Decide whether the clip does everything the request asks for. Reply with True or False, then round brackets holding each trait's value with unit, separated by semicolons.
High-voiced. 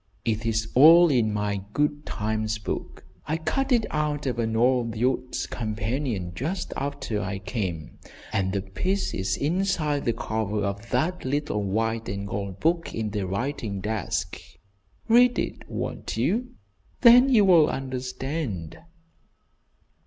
False (115 Hz)